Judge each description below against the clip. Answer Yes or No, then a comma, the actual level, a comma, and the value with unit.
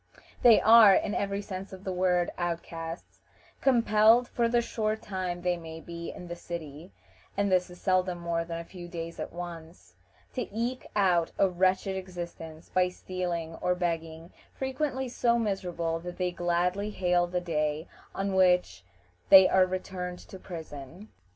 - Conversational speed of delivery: Yes, average, 160 wpm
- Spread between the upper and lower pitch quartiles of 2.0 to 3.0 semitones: Yes, narrow, 2.6 semitones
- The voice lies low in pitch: No, medium, 180 Hz